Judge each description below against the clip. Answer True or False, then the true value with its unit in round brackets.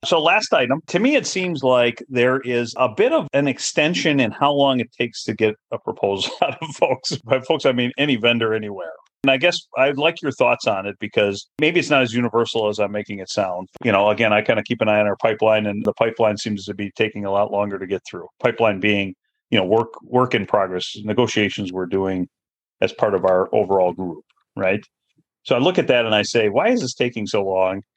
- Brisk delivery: True (240 wpm)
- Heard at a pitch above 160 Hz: False (115 Hz)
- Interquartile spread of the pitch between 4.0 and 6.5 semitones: True (4.3 semitones)